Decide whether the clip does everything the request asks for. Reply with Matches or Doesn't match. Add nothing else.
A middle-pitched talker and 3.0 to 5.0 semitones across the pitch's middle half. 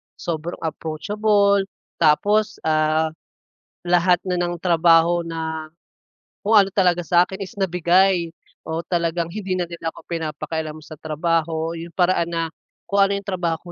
Doesn't match